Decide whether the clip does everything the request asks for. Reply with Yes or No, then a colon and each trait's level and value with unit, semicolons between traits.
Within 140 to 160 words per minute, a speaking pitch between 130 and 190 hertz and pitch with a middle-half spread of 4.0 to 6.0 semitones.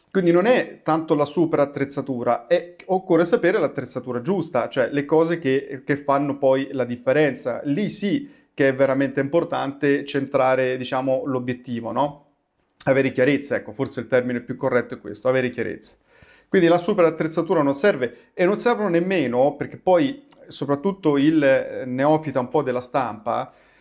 Yes: average, 155 wpm; medium, 140 Hz; average, 4.5 semitones